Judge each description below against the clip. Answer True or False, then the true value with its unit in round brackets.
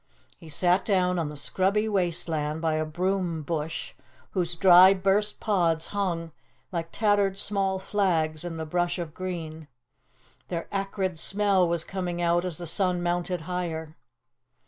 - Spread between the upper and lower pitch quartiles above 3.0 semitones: False (2.7 semitones)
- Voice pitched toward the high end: False (175 Hz)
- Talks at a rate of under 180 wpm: True (150 wpm)